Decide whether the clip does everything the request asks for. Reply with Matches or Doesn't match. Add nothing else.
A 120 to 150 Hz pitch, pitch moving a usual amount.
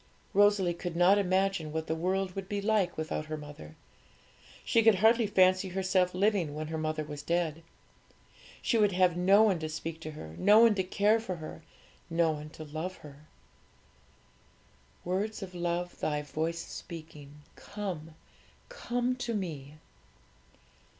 Doesn't match